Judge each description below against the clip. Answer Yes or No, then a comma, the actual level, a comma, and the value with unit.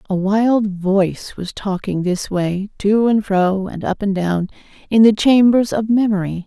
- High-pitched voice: Yes, high, 200 Hz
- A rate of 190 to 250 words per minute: No, average, 175 wpm